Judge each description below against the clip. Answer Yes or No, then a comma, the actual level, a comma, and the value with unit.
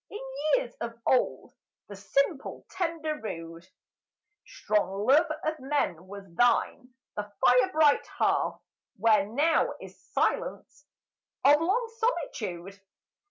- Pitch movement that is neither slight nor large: No, wide, 7.6 semitones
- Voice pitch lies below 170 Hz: No, very high, 250 Hz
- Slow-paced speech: Yes, slow, 115 wpm